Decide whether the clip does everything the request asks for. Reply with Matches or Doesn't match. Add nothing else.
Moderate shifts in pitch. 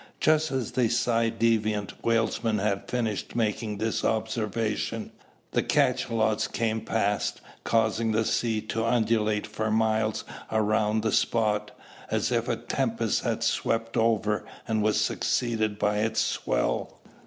Doesn't match